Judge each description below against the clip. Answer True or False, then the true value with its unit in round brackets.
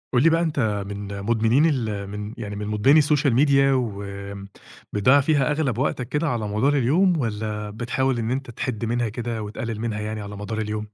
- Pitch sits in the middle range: False (115 Hz)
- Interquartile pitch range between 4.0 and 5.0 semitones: True (4.5 semitones)